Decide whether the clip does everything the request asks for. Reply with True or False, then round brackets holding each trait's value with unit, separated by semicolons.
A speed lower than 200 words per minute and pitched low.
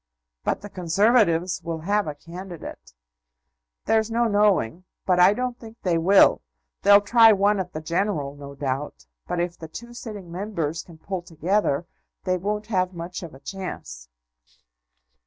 False (155 wpm; 185 Hz)